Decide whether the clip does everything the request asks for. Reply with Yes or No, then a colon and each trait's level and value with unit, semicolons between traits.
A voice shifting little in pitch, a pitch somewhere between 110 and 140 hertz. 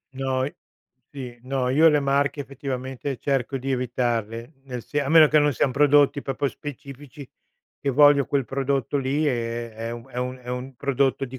Yes: narrow, 2.1 semitones; low, 135 Hz